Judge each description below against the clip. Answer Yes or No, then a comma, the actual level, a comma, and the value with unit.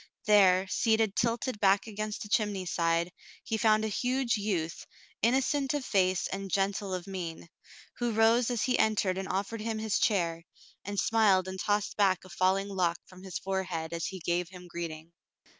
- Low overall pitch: No, high, 195 Hz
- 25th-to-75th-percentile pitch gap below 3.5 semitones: Yes, average, 3.1 semitones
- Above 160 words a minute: Yes, average, 175 wpm